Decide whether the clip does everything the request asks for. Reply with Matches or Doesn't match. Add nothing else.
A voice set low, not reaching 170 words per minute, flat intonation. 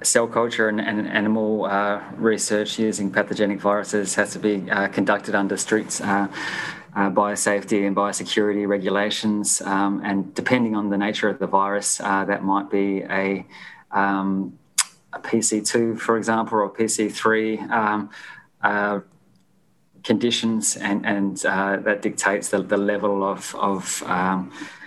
Matches